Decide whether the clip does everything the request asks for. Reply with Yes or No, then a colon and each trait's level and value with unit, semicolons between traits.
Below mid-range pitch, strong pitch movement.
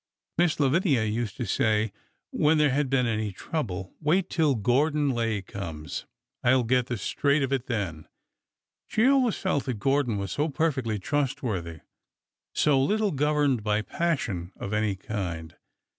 Yes: low, 125 Hz; wide, 6.0 semitones